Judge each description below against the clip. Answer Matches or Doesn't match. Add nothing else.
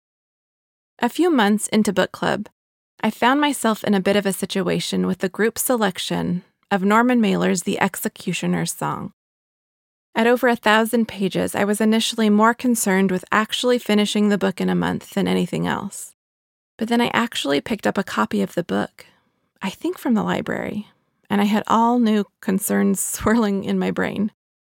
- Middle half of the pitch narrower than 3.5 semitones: Matches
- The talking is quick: Doesn't match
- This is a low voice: Doesn't match